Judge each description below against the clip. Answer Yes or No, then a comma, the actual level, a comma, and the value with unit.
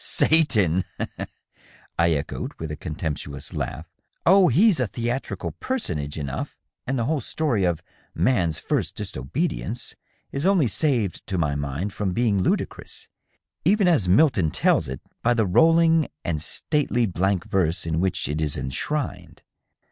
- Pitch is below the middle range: Yes, very low, 95 Hz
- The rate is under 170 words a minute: Yes, average, 160 wpm